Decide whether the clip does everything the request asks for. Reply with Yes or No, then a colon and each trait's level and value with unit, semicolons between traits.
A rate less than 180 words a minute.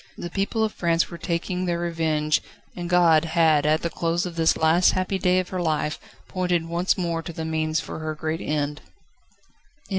No: average, 190 wpm